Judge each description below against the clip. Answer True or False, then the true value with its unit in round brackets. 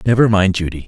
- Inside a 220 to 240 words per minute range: False (205 wpm)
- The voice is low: True (100 Hz)